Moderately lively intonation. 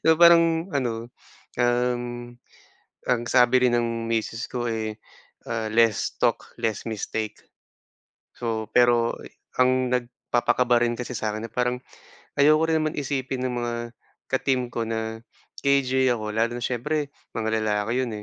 No: narrow, 2.2 semitones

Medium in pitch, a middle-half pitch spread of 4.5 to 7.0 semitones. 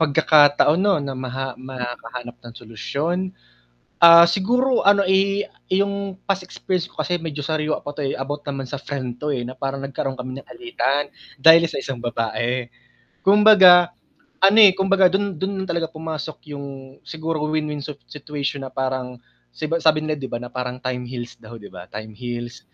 Yes: medium, 145 Hz; wide, 5.6 semitones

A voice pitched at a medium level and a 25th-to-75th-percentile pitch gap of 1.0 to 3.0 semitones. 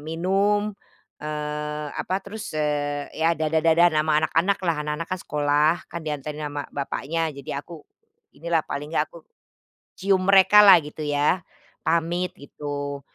Yes: medium, 155 Hz; narrow, 2.4 semitones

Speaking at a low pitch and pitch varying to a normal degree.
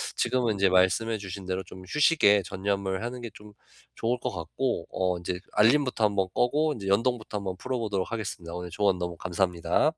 Yes: low, 100 Hz; average, 3.9 semitones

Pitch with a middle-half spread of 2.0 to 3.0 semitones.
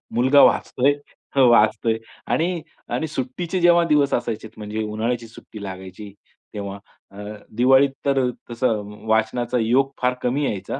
No: average, 4.2 semitones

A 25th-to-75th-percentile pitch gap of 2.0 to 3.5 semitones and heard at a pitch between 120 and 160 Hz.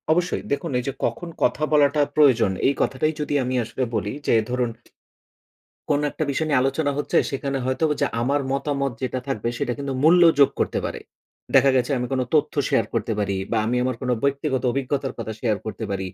Yes: average, 2.7 semitones; low, 135 Hz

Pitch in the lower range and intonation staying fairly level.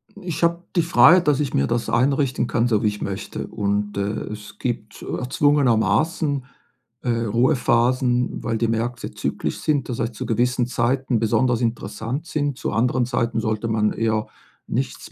No: low, 120 Hz; average, 3.3 semitones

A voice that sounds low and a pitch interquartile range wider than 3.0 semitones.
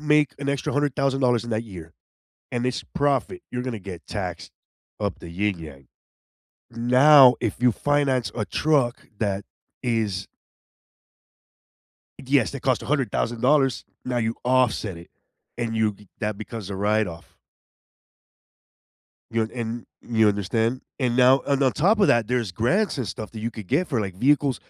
Yes: low, 120 Hz; average, 4.3 semitones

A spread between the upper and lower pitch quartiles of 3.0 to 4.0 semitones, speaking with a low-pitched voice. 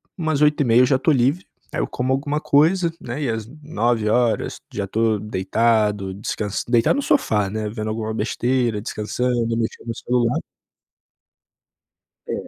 Yes: average, 3.5 semitones; low, 115 Hz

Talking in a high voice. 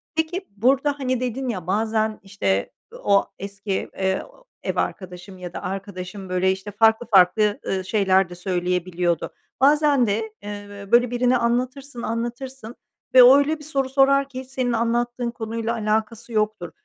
Yes: high, 220 Hz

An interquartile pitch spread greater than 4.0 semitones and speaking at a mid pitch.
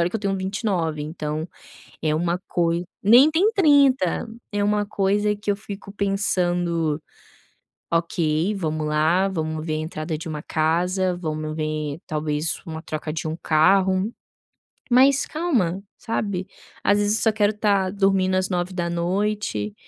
Yes: average, 4.4 semitones; medium, 180 Hz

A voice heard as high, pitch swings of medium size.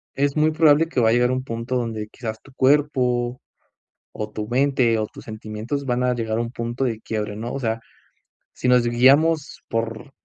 No: low, 120 Hz; average, 3.0 semitones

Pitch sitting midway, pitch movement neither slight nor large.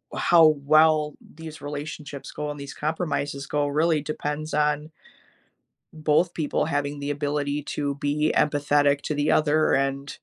No: medium, 150 Hz; narrow, 1.2 semitones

